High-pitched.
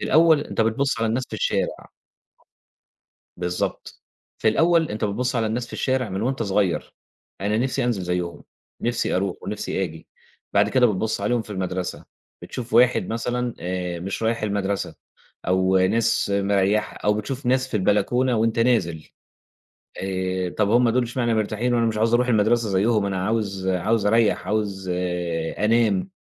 No: low, 110 Hz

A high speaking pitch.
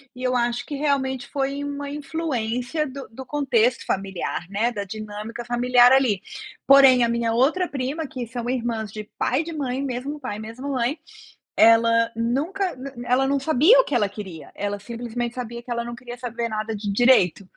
Yes: high, 245 Hz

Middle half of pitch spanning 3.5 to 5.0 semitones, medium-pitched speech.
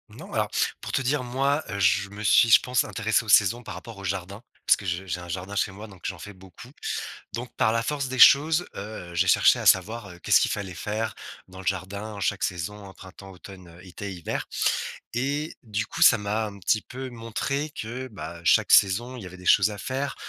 No: average, 4.1 semitones; low, 105 Hz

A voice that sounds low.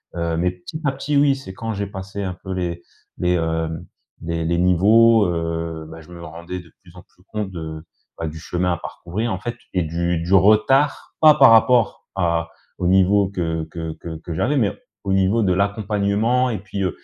Yes: very low, 90 Hz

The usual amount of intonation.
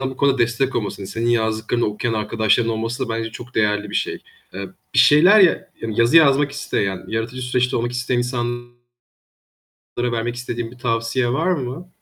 No: narrow, 2.2 semitones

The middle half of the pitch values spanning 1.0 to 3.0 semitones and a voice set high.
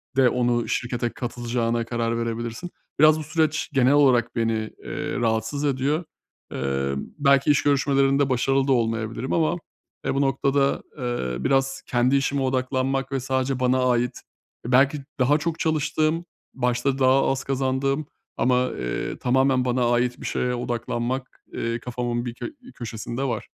No: narrow, 2.4 semitones; low, 130 Hz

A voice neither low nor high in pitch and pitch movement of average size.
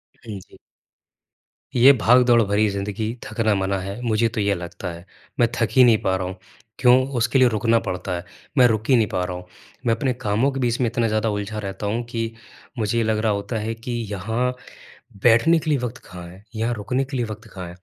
No: low, 110 Hz; average, 3.2 semitones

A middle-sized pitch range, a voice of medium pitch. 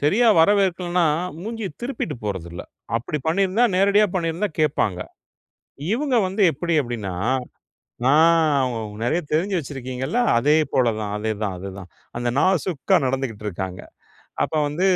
No: wide, 7.9 semitones; medium, 150 Hz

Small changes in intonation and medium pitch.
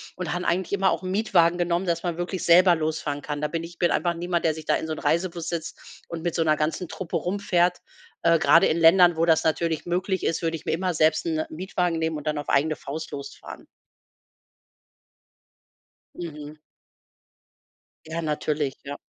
Yes: narrow, 1.9 semitones; medium, 165 Hz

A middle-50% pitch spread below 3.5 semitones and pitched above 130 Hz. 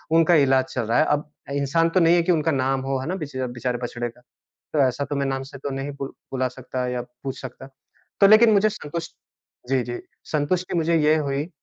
No: average, 4.2 semitones; medium, 140 Hz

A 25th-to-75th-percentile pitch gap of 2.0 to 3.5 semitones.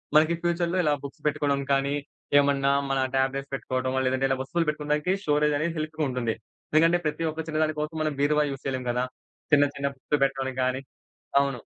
Yes: narrow, 2.4 semitones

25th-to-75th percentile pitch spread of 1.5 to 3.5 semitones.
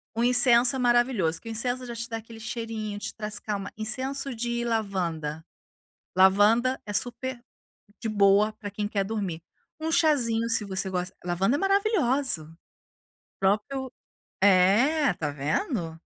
No: average, 4.2 semitones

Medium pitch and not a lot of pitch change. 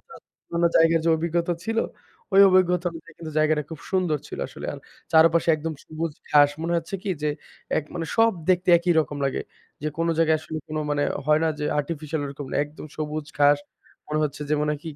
Yes: medium, 160 Hz; narrow, 2.0 semitones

